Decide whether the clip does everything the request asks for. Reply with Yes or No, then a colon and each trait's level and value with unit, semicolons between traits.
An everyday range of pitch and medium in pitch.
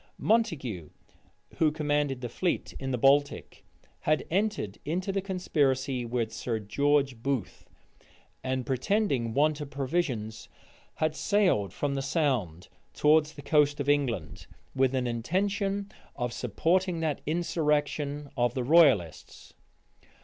Yes: average, 4.5 semitones; medium, 145 Hz